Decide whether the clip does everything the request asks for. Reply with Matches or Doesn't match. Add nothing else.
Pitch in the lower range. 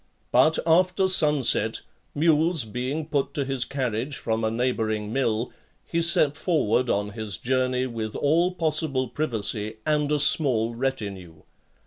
Matches